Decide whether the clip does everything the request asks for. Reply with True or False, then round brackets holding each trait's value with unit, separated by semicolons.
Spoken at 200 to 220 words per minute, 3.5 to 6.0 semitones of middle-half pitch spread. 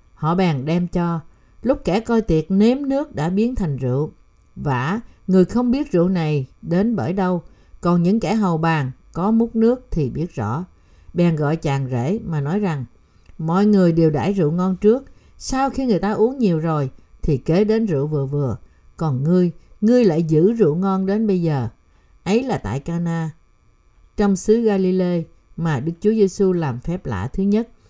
False (185 wpm; 5.2 semitones)